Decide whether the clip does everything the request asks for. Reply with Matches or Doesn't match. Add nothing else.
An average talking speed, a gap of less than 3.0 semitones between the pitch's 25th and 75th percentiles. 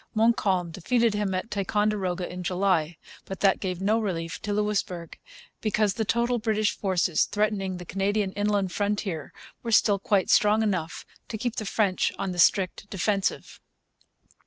Matches